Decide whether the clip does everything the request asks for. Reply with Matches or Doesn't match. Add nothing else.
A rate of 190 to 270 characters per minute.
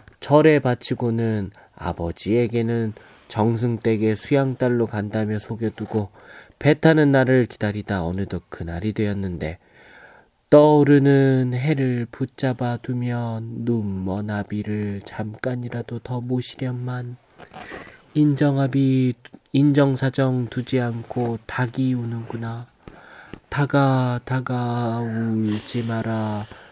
Matches